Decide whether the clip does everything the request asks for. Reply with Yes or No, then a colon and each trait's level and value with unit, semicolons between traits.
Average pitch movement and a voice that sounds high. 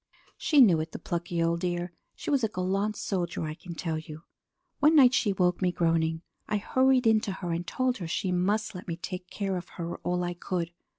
No: average, 3.7 semitones; medium, 180 Hz